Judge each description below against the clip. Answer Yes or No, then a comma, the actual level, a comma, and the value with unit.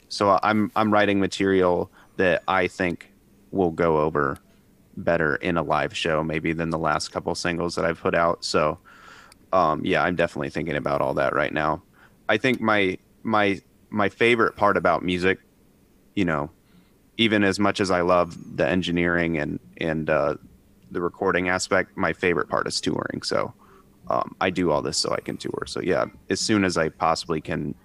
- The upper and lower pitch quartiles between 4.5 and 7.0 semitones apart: No, average, 3.1 semitones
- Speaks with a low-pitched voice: Yes, very low, 90 Hz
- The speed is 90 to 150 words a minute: No, average, 185 wpm